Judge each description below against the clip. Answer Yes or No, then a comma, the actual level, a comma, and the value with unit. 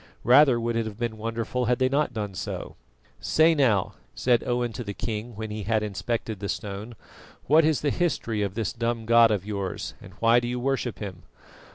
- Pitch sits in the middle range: No, low, 115 Hz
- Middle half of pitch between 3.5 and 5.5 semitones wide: No, average, 2.7 semitones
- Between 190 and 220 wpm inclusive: Yes, fast, 205 wpm